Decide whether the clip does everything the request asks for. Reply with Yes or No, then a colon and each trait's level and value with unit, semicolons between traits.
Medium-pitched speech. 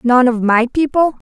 No: very high, 255 Hz